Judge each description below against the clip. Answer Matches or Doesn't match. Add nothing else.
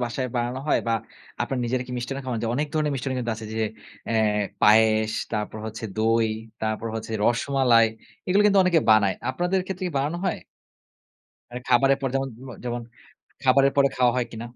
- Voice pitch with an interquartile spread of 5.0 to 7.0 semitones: Doesn't match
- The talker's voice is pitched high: Doesn't match